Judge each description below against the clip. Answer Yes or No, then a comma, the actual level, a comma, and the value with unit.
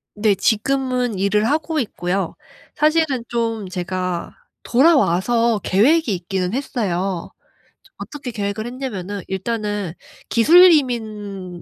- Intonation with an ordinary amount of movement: Yes, average, 5.0 semitones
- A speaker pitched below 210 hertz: No, high, 215 Hz